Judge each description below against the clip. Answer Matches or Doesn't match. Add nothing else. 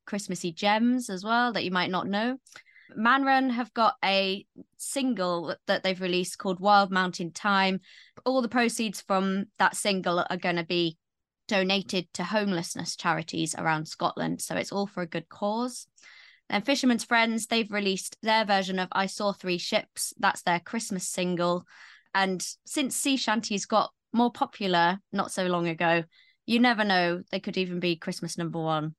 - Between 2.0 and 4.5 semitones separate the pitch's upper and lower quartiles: Matches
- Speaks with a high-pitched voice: Matches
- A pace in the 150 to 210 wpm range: Matches